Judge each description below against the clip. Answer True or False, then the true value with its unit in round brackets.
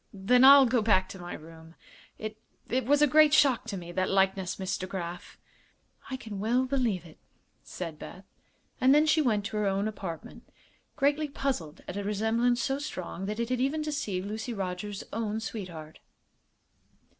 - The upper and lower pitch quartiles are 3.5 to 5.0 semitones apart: False (5.5 semitones)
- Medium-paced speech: True (175 wpm)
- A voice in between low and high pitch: False (215 Hz)